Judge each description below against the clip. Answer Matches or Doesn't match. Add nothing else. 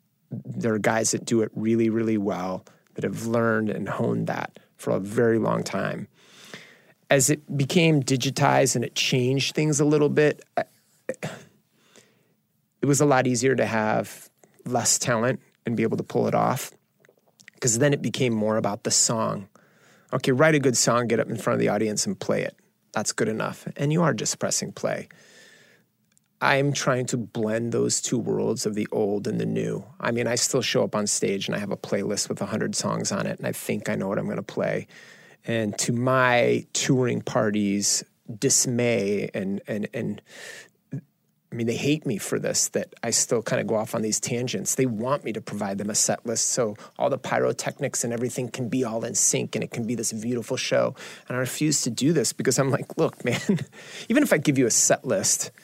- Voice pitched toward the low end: Matches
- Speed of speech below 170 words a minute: Doesn't match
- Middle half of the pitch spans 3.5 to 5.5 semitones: Matches